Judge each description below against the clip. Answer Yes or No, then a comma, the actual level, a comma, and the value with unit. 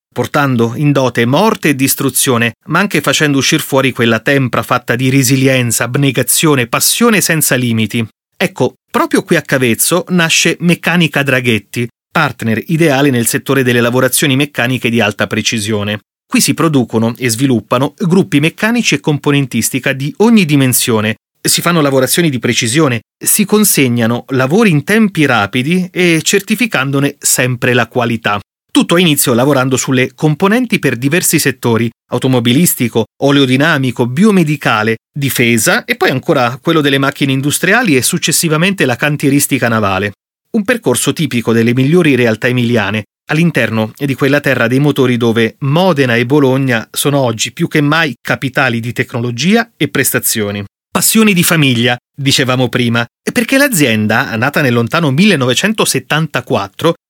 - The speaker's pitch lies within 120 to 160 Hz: Yes, low, 135 Hz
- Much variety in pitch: No, average, 4.8 semitones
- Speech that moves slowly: No, average, 135 wpm